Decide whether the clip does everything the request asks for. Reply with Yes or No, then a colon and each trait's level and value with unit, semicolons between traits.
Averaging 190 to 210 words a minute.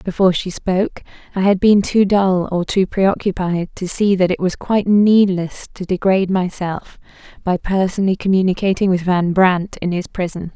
No: average, 170 wpm